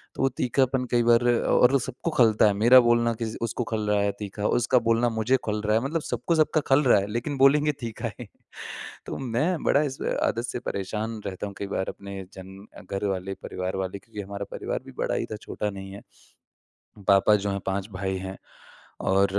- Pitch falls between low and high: No, low, 110 Hz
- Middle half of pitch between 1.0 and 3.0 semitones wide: No, average, 4.0 semitones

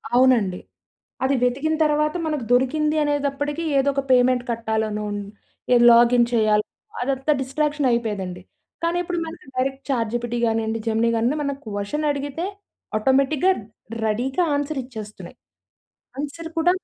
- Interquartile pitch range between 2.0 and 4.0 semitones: No, average, 4.5 semitones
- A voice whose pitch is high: Yes, very high, 260 Hz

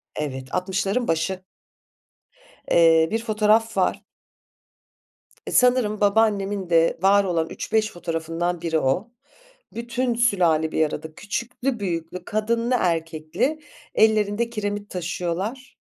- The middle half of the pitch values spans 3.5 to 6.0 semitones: Yes, average, 5.0 semitones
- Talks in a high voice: Yes, high, 195 Hz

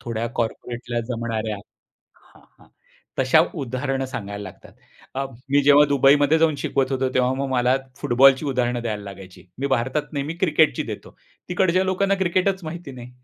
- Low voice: Yes, low, 130 Hz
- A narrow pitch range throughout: No, average, 3.7 semitones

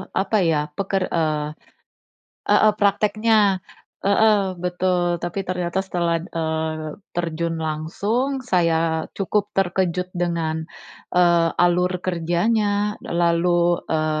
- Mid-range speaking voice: Yes, medium, 175 Hz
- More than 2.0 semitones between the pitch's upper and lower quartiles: Yes, average, 2.8 semitones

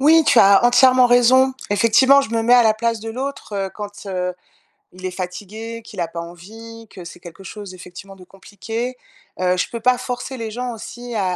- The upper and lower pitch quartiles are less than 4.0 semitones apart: No, average, 4.5 semitones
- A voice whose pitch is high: Yes, high, 225 Hz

